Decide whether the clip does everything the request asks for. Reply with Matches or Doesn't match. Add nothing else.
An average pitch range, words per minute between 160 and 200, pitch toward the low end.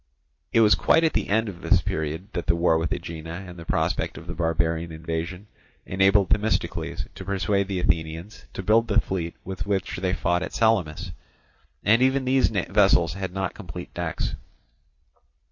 Matches